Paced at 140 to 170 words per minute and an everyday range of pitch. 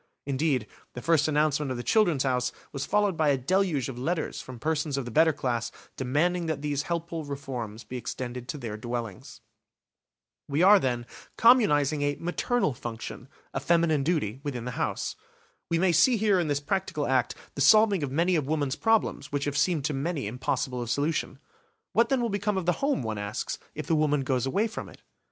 No: average, 195 wpm; average, 4.9 semitones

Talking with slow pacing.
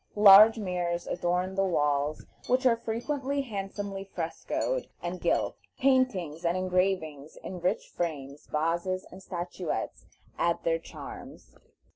Yes: slow, 120 wpm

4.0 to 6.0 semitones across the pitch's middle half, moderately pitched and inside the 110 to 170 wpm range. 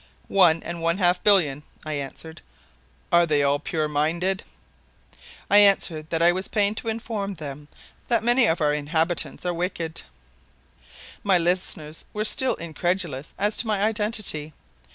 Yes: average, 4.6 semitones; medium, 175 Hz; average, 150 wpm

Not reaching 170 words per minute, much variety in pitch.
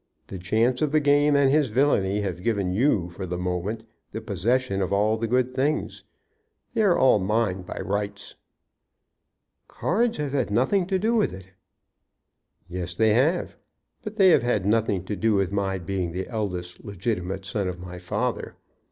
No: average, 175 wpm; wide, 5.8 semitones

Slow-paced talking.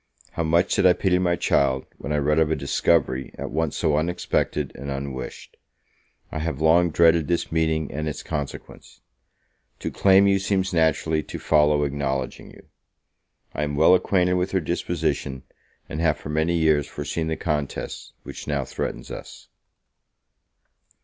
No: average, 160 wpm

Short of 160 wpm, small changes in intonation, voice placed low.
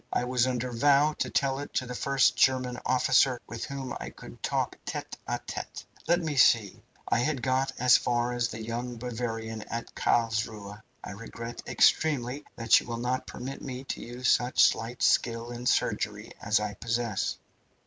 No: average, 180 wpm; narrow, 2.0 semitones; low, 120 Hz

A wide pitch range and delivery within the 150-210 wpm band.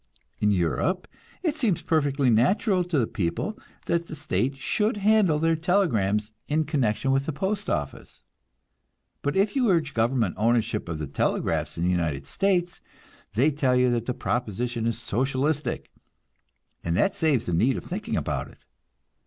Yes: wide, 7.3 semitones; average, 160 wpm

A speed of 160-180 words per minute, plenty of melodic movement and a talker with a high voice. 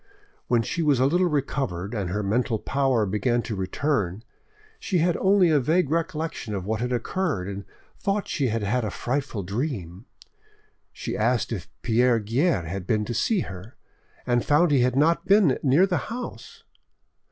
No: average, 175 wpm; wide, 6.9 semitones; low, 125 Hz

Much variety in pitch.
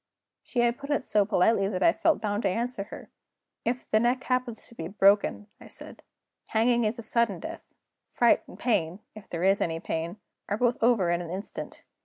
No: average, 3.7 semitones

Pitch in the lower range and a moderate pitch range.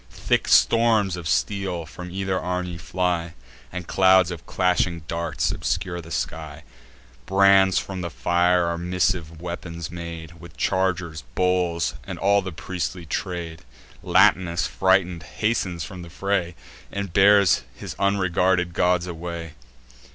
No: very low, 90 Hz; narrow, 1.9 semitones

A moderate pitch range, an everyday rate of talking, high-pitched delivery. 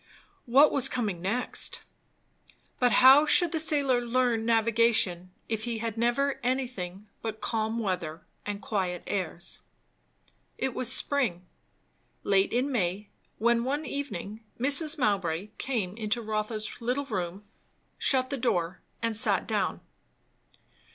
No: average, 4.2 semitones; slow, 125 wpm; high, 230 Hz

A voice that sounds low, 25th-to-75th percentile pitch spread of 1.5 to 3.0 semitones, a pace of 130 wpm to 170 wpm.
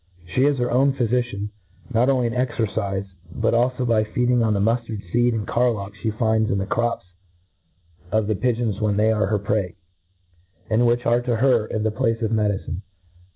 No: low, 115 Hz; narrow, 2.5 semitones; average, 195 wpm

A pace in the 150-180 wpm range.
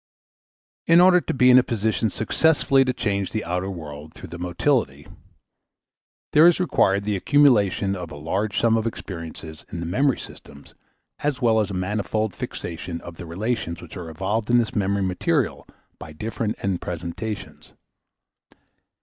Yes: average, 160 wpm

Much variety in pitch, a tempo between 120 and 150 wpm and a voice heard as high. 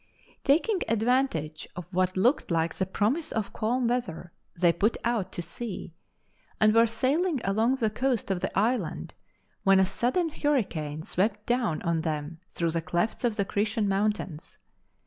No: wide, 5.8 semitones; average, 160 wpm; high, 210 Hz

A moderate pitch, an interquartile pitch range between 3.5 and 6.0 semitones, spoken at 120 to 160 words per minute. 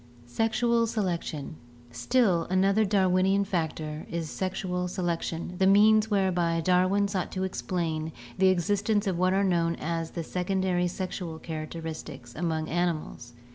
No: medium, 180 Hz; average, 2.8 semitones; slow, 135 wpm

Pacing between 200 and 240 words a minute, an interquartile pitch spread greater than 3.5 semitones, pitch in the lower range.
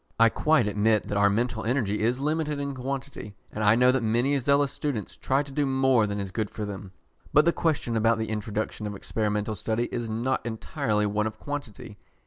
Yes: fast, 205 wpm; average, 4.2 semitones; low, 115 Hz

